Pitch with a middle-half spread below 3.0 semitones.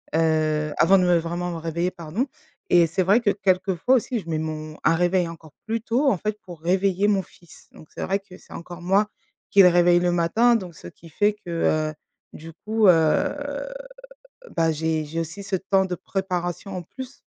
No: average, 3.3 semitones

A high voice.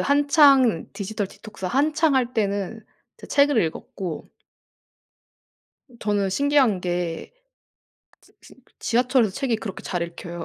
Yes: high, 220 Hz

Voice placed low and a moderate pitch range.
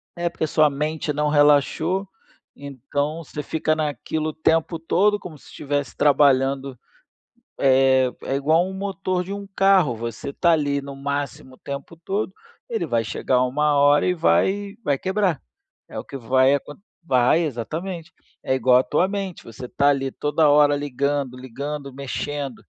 No: medium, 145 Hz; average, 3.4 semitones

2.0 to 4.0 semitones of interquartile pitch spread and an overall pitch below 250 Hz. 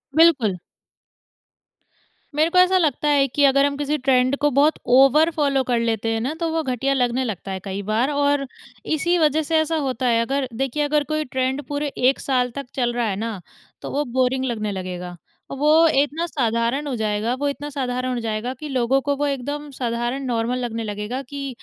No: average, 3.7 semitones; very high, 265 Hz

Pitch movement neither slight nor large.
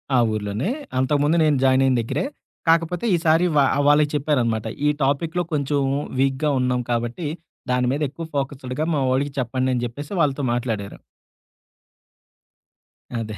Yes: average, 3.1 semitones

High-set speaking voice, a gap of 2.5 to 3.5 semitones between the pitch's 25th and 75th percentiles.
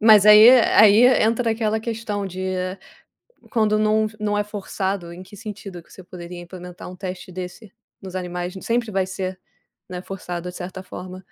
Yes: high, 195 Hz; average, 2.9 semitones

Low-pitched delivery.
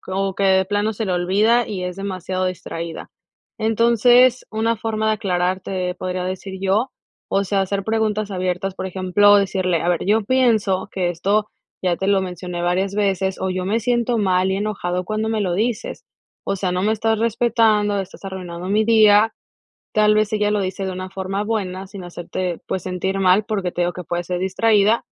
No: high, 195 Hz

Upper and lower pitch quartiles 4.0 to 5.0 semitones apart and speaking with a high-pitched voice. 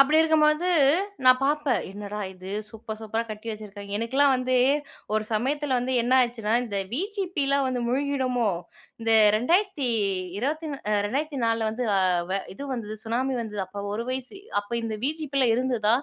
Yes: average, 4.5 semitones; very high, 250 Hz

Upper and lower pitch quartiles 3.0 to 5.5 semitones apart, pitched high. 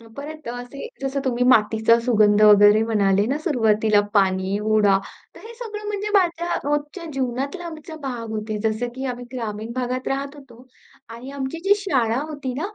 Yes: average, 5.1 semitones; very high, 250 Hz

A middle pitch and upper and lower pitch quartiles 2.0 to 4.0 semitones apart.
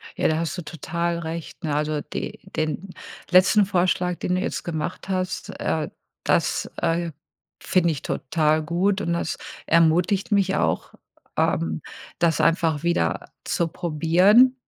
Yes: medium, 170 Hz; narrow, 2.6 semitones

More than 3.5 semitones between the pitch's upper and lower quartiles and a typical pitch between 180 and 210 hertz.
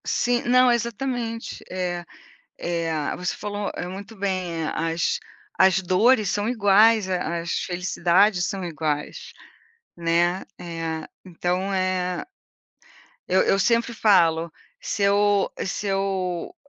No: average, 3.0 semitones; medium, 185 Hz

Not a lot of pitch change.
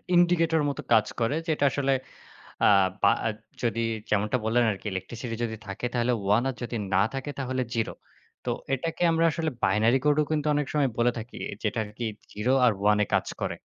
No: average, 4.8 semitones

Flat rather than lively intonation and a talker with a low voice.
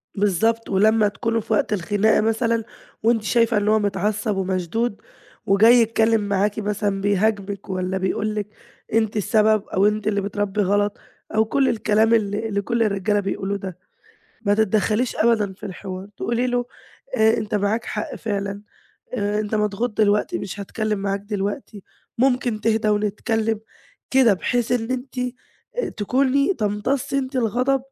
No: narrow, 2.1 semitones; high, 215 Hz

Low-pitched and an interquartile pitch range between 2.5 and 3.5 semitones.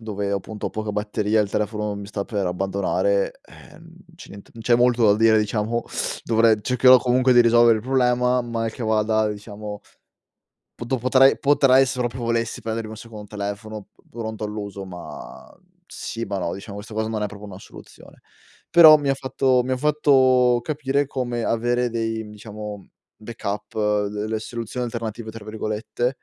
Yes: low, 115 Hz; average, 2.9 semitones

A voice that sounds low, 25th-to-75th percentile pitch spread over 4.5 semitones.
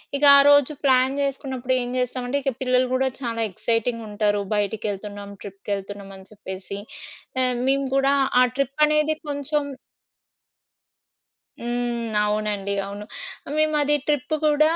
No: high, 245 Hz; average, 5.0 semitones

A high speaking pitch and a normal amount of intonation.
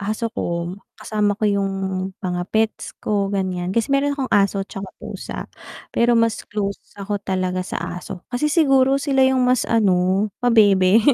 Yes: high, 205 Hz; average, 3.8 semitones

